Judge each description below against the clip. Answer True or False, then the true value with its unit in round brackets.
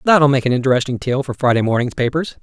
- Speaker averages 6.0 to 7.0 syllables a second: True (6.5 syllables/s)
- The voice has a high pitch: False (135 Hz)